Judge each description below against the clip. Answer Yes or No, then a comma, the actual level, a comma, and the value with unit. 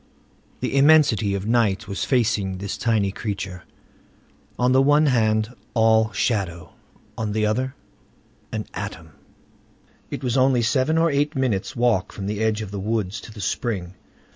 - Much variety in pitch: No, average, 4.2 semitones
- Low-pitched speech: Yes, low, 110 Hz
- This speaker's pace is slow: No, average, 155 wpm